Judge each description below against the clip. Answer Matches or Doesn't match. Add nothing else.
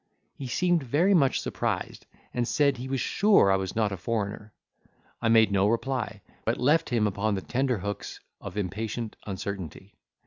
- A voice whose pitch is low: Matches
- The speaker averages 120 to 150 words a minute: Doesn't match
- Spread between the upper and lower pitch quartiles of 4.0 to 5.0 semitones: Matches